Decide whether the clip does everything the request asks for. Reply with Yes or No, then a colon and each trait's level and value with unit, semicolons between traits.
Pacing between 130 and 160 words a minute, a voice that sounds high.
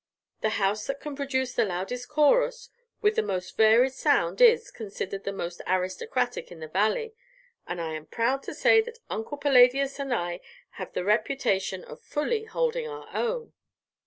No: average, 170 wpm; very high, 250 Hz